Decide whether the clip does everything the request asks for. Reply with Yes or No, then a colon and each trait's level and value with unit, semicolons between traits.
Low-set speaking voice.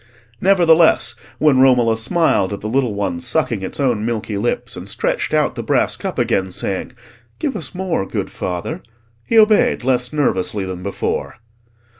Yes: low, 120 Hz